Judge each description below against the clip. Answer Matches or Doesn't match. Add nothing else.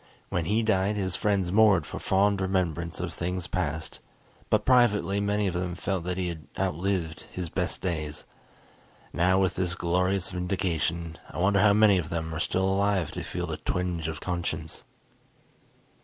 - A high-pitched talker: Doesn't match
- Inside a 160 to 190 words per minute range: Matches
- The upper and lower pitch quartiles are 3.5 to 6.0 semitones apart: Doesn't match